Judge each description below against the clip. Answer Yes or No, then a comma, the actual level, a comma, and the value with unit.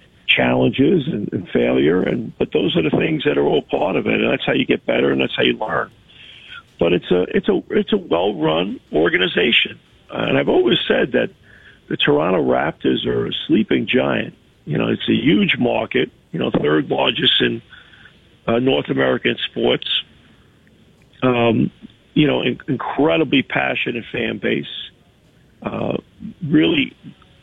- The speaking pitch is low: Yes, low, 130 Hz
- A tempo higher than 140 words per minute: Yes, average, 160 wpm